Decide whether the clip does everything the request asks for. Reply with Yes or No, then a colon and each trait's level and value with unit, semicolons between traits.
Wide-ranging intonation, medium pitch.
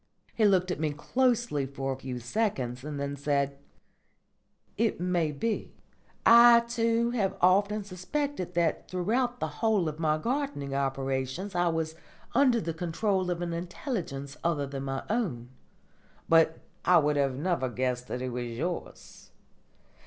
Yes: wide, 7.3 semitones; medium, 170 Hz